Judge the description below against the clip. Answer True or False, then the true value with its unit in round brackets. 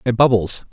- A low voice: True (115 Hz)